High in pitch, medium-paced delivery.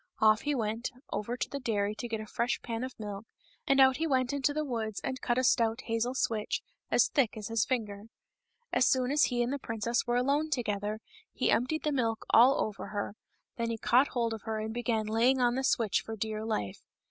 No: high, 235 Hz; fast, 225 wpm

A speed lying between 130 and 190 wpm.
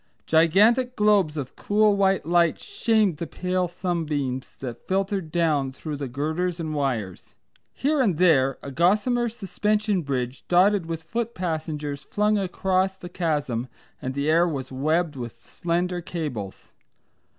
Yes: average, 140 wpm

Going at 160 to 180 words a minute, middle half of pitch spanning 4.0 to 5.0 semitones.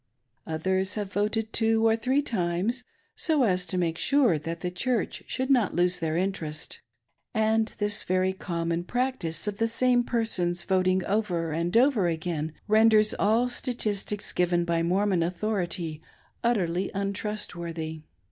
No: average, 145 wpm; average, 4.5 semitones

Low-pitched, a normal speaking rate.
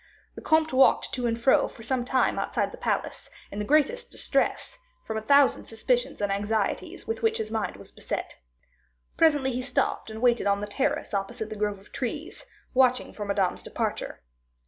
No: high, 240 Hz; average, 185 wpm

